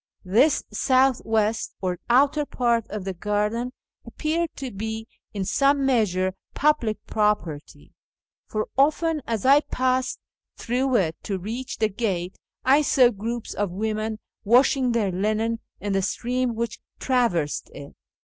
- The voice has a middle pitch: No, high, 225 Hz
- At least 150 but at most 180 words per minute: No, average, 140 wpm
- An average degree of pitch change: Yes, average, 3.9 semitones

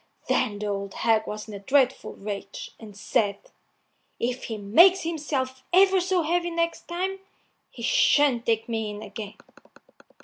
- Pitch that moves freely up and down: Yes, wide, 8.2 semitones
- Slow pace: No, average, 150 wpm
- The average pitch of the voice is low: No, high, 245 Hz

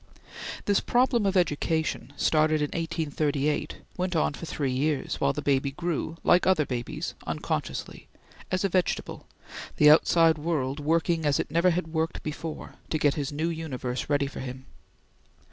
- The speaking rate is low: No, average, 160 wpm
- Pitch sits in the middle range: Yes, medium, 155 Hz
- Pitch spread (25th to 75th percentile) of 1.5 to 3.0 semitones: Yes, average, 2.7 semitones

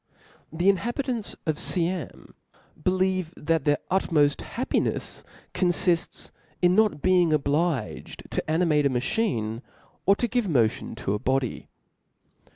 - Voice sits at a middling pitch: Yes, medium, 170 Hz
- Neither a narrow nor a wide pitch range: Yes, average, 4.6 semitones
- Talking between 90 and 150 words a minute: Yes, average, 140 wpm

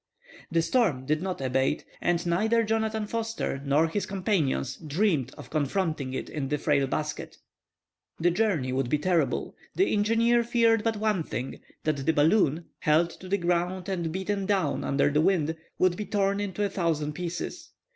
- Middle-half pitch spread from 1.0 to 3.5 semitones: No, wide, 5.4 semitones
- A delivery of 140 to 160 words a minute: No, average, 170 wpm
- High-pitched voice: No, medium, 175 Hz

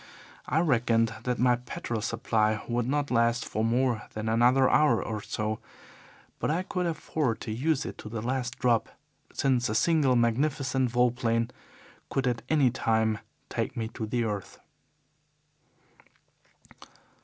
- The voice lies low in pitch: Yes, low, 120 Hz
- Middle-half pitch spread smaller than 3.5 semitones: Yes, average, 2.7 semitones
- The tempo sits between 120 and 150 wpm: Yes, average, 145 wpm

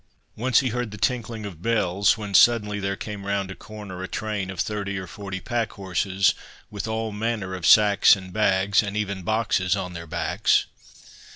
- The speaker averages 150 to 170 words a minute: No, average, 185 wpm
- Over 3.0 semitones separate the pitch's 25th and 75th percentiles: No, narrow, 2.4 semitones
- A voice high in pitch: No, low, 100 Hz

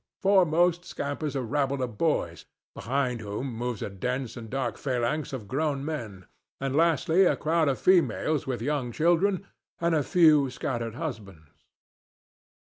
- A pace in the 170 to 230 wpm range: No, average, 145 wpm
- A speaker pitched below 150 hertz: Yes, medium, 140 Hz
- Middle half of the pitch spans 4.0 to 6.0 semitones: Yes, average, 4.8 semitones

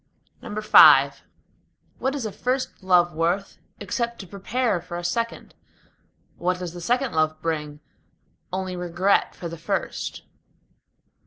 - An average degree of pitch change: Yes, average, 4.5 semitones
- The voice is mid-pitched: Yes, medium, 180 Hz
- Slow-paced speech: Yes, slow, 130 wpm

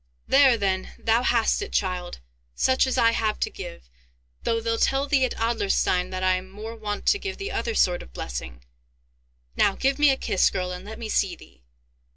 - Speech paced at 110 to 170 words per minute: No, average, 200 wpm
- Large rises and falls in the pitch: Yes, wide, 5.9 semitones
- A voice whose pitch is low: No, high, 220 Hz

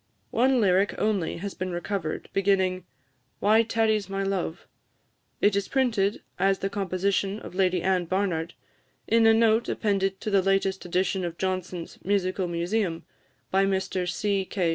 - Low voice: No, high, 195 Hz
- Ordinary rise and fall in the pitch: No, narrow, 1.8 semitones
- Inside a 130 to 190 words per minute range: Yes, average, 150 wpm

